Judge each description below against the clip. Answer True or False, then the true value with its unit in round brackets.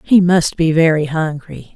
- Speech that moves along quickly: False (170 wpm)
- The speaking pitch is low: False (160 Hz)